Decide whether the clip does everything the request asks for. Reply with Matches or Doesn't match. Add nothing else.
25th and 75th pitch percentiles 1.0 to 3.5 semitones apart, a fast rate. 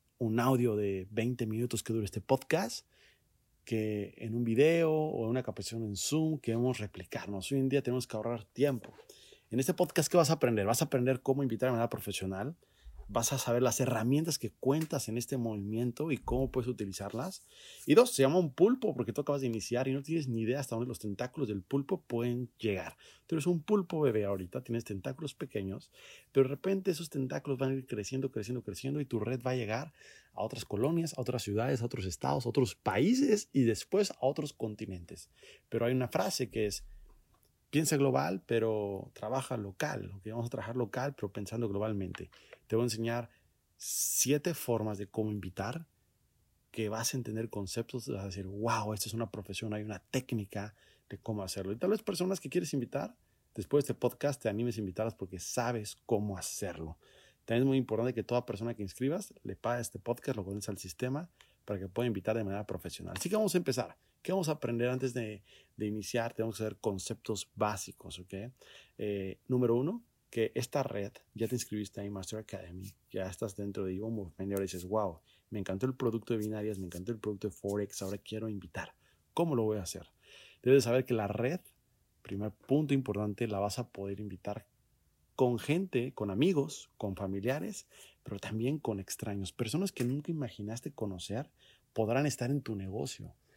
Doesn't match